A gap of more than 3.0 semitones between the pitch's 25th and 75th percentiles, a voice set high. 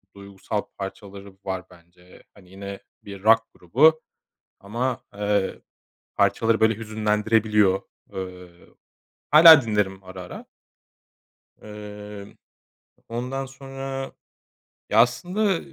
No: average, 3.8 semitones; low, 105 Hz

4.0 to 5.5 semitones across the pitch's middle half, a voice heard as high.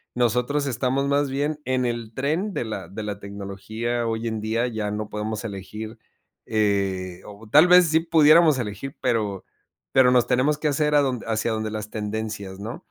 No: average, 4.4 semitones; low, 115 Hz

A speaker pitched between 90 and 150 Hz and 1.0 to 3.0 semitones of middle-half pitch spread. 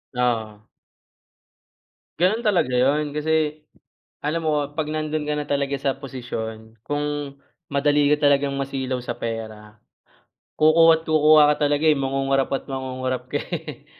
Yes: medium, 140 Hz; average, 2.7 semitones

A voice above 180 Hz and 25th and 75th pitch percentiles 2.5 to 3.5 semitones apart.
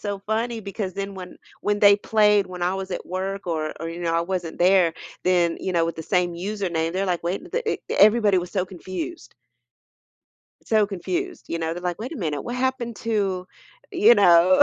Yes: high, 190 Hz; average, 3.2 semitones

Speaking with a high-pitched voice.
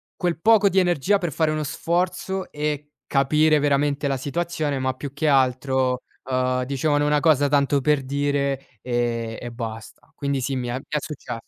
No: medium, 140 Hz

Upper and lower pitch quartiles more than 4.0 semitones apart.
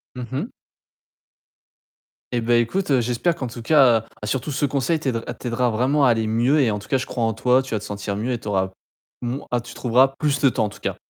No: average, 2.9 semitones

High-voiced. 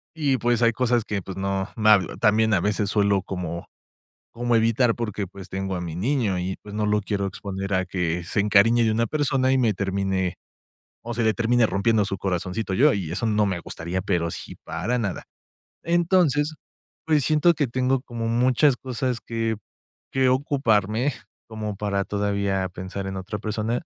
No: low, 105 Hz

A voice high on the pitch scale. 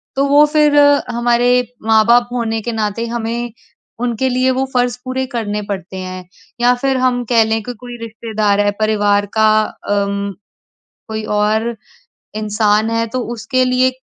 Yes: high, 230 Hz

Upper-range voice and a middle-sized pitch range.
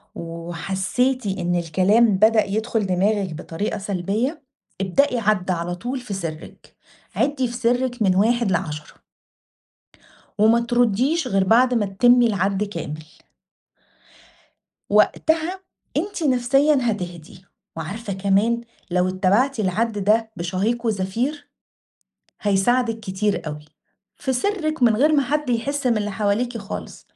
Yes: high, 215 Hz; average, 4.6 semitones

